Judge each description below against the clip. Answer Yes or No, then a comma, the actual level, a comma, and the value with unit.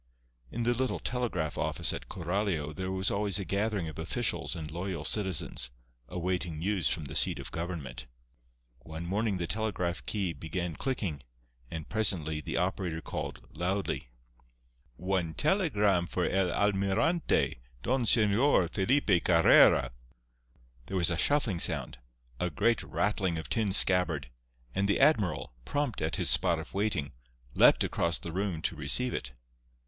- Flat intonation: No, average, 4.1 semitones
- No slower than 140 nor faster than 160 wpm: Yes, average, 145 wpm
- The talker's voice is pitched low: Yes, very low, 95 Hz